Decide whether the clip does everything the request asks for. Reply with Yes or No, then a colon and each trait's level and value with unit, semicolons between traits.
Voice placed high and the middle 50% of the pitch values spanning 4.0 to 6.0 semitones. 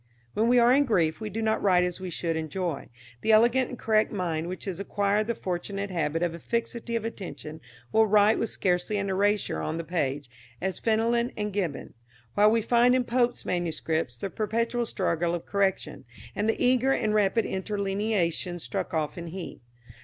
Yes: high, 200 Hz; average, 4.3 semitones